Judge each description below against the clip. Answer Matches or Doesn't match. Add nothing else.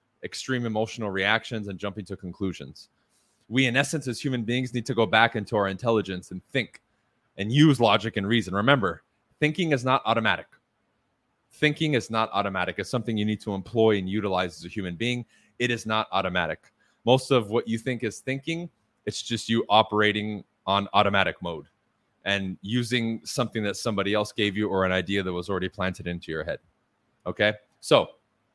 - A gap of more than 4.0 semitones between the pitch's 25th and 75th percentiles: Doesn't match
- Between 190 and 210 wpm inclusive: Doesn't match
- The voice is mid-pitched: Doesn't match